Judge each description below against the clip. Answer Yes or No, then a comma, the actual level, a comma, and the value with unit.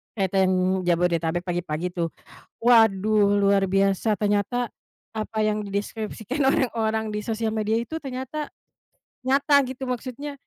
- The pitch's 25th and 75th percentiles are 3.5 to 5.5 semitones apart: Yes, average, 4.1 semitones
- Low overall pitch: No, high, 215 Hz